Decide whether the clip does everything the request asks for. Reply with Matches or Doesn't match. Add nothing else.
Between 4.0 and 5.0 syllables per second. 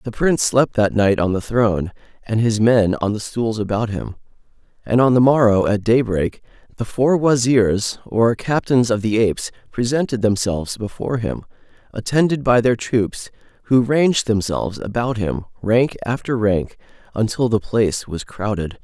Matches